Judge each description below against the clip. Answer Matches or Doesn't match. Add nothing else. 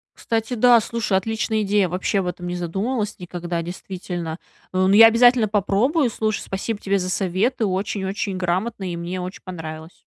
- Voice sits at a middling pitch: Doesn't match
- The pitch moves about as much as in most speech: Matches